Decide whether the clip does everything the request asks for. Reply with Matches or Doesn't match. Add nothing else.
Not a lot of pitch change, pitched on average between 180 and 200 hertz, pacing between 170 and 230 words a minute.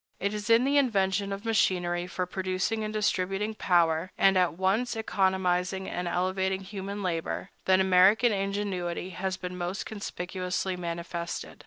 Doesn't match